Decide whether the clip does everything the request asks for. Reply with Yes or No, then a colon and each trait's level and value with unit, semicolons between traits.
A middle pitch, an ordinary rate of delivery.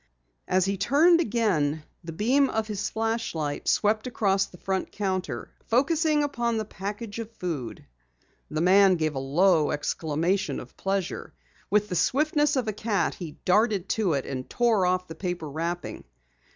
No: high, 195 Hz; average, 160 wpm